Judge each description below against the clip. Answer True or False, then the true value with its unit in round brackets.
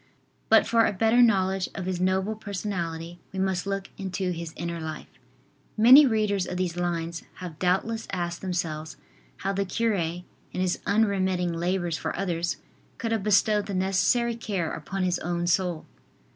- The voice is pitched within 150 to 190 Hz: True (185 Hz)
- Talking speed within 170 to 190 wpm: False (160 wpm)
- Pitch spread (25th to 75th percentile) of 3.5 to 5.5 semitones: False (2.7 semitones)